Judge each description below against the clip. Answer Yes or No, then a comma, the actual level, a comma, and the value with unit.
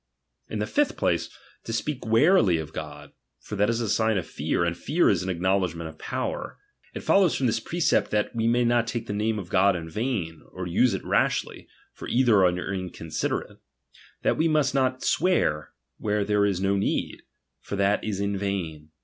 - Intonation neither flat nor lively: Yes, average, 4.7 semitones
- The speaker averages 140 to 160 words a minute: No, average, 195 wpm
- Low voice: Yes, low, 100 Hz